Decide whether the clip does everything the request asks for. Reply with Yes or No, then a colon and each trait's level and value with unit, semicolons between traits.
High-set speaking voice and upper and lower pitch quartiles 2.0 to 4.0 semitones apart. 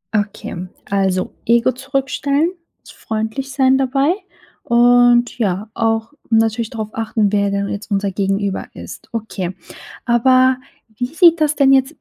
No: high, 235 Hz; average, 4.4 semitones